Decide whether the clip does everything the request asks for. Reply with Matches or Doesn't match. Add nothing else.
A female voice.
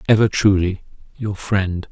Doesn't match